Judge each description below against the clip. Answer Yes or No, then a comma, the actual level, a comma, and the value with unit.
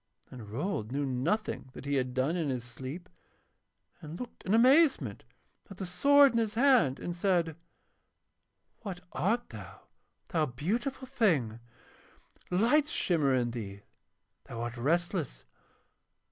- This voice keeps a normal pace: No, slow, 130 wpm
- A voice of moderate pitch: Yes, medium, 170 Hz